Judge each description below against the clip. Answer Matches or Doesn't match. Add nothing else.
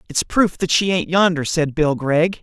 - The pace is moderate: Doesn't match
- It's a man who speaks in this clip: Matches